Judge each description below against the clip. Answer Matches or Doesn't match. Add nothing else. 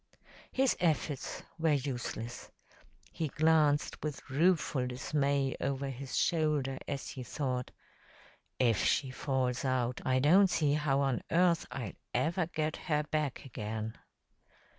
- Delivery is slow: Matches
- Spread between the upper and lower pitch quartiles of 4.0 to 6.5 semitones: Doesn't match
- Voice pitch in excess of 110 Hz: Matches